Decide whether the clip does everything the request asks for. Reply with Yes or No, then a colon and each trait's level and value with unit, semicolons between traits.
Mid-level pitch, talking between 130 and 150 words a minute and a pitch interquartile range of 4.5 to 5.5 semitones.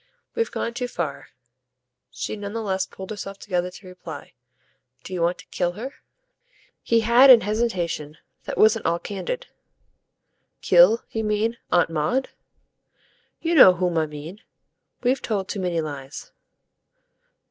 No: high, 195 Hz; average, 145 wpm; average, 4.8 semitones